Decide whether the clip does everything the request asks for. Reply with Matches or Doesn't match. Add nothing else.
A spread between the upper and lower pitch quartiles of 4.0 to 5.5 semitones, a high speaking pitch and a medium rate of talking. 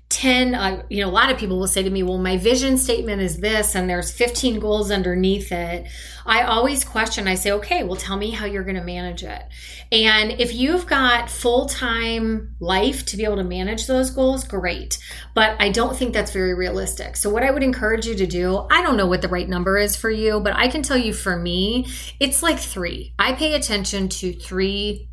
Doesn't match